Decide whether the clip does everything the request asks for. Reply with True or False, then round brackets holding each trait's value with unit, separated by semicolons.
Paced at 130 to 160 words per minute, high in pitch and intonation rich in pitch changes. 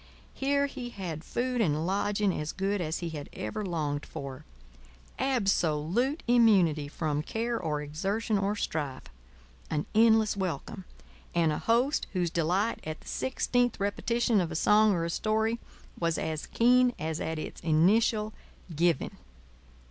True (145 wpm; 195 Hz; 6.2 semitones)